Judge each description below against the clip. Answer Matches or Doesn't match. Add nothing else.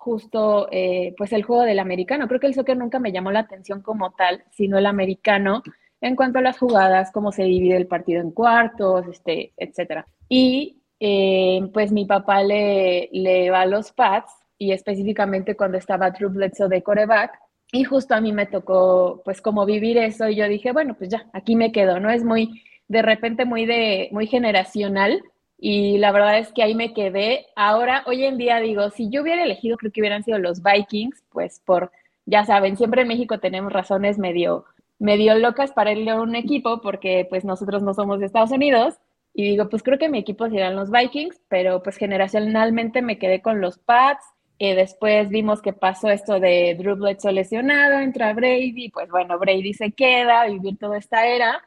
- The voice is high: Matches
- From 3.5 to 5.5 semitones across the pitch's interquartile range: Doesn't match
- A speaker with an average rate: Doesn't match